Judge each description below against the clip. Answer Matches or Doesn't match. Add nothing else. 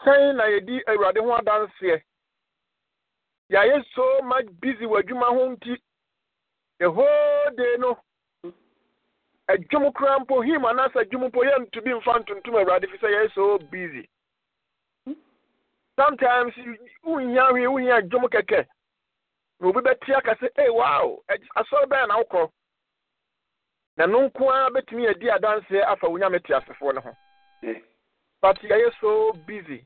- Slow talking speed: Matches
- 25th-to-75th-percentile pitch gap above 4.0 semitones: Matches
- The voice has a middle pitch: Doesn't match